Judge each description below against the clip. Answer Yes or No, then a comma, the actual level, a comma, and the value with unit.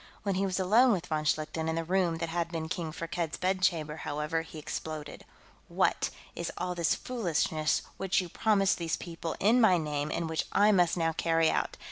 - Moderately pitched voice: Yes, medium, 165 Hz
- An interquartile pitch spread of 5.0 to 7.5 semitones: No, average, 2.7 semitones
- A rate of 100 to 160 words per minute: No, average, 195 wpm